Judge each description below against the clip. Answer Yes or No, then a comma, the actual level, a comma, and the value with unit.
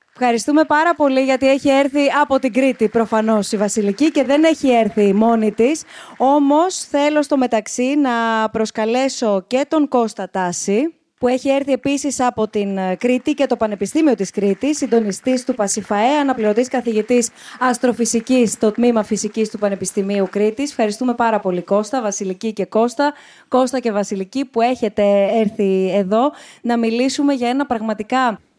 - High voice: Yes, high, 235 Hz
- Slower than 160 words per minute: Yes, average, 150 wpm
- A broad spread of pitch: No, average, 4.1 semitones